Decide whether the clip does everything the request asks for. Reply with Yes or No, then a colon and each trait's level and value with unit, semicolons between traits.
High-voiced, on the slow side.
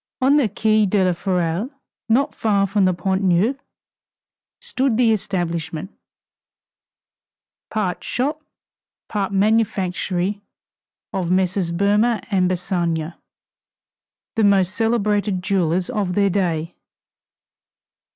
Yes: high, 195 Hz; slow, 100 wpm